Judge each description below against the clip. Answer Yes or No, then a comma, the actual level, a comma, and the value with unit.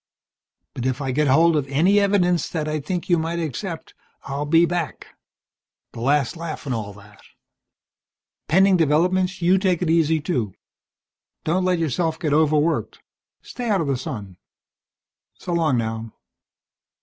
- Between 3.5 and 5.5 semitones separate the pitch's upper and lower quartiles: Yes, average, 4.3 semitones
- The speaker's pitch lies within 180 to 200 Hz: No, medium, 160 Hz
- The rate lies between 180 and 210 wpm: No, average, 150 wpm